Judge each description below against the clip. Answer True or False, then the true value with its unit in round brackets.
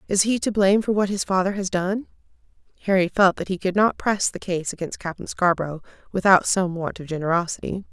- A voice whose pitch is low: False (190 Hz)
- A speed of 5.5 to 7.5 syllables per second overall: True (5.9 syllables/s)